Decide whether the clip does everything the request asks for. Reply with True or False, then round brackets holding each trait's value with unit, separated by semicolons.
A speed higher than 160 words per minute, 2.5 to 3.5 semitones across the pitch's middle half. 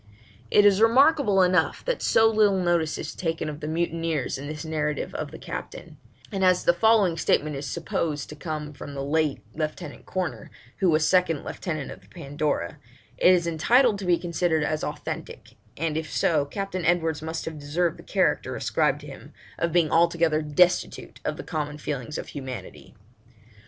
True (180 wpm; 3.1 semitones)